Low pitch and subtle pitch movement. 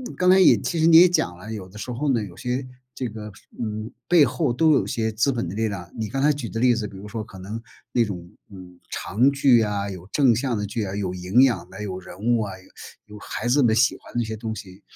No: low, 110 Hz; average, 3.9 semitones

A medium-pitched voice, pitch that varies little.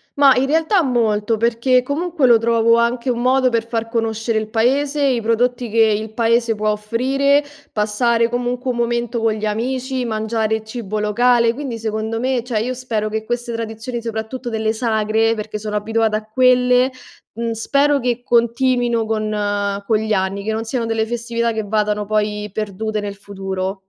No: high, 230 Hz; narrow, 2.3 semitones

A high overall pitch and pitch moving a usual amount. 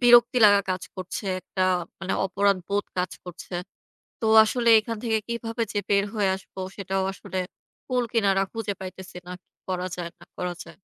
Yes: high, 200 Hz; average, 3.4 semitones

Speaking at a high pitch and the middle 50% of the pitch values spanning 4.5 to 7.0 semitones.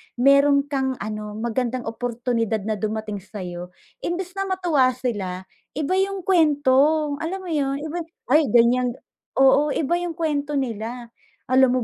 Yes: very high, 260 Hz; average, 5.1 semitones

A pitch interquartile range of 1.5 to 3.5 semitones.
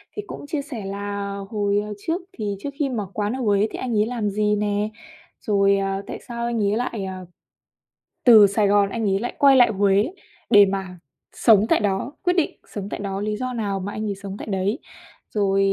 Yes: average, 2.9 semitones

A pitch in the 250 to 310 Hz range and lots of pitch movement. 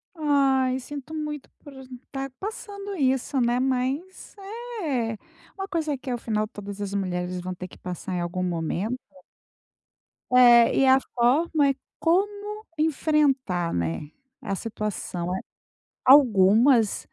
Yes: very high, 255 Hz; wide, 7.0 semitones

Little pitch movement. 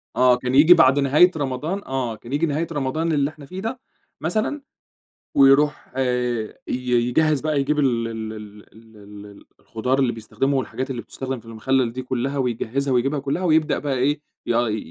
No: average, 3.5 semitones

